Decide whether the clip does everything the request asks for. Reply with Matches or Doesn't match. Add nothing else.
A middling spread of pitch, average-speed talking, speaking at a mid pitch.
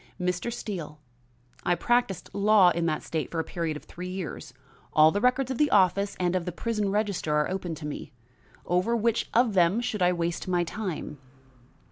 Matches